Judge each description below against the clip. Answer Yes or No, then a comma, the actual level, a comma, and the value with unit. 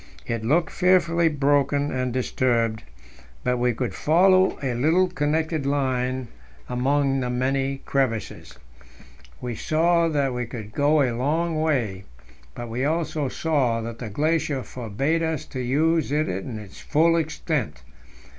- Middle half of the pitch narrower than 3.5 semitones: No, average, 4.3 semitones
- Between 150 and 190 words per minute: No, average, 140 wpm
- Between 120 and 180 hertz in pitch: Yes, low, 135 Hz